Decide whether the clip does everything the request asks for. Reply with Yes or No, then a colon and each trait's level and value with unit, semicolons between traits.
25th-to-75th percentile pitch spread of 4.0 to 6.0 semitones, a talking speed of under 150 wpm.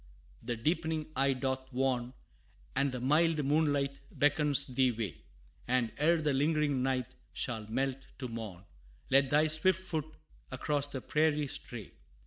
No: average, 3.1 semitones; average, 140 wpm